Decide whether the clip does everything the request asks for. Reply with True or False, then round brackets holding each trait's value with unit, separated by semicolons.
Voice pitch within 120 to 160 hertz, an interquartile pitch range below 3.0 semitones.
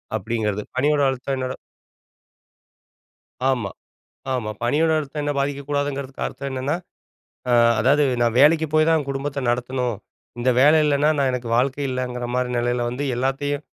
True (135 Hz; 2.6 semitones)